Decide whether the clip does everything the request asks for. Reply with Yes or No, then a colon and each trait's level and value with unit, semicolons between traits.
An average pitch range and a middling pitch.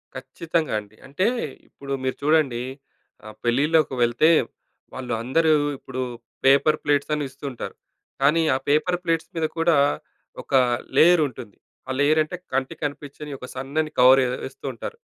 Yes: average, 3.3 semitones; medium, 145 Hz